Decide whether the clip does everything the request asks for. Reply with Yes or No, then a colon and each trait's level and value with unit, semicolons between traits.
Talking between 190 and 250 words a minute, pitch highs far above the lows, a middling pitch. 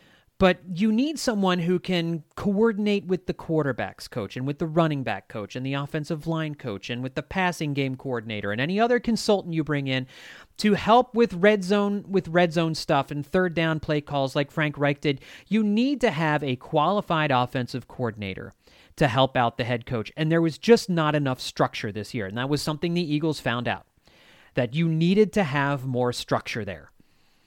Yes: average, 200 wpm; wide, 5.9 semitones; medium, 155 Hz